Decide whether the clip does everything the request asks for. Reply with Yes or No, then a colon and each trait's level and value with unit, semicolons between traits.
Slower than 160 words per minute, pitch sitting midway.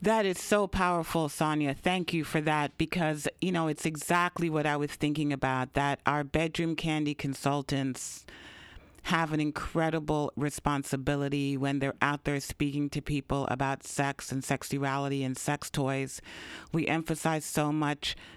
Yes: average, 150 wpm; medium, 145 Hz